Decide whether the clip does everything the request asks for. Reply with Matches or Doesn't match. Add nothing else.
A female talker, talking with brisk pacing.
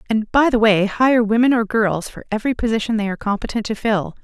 Matches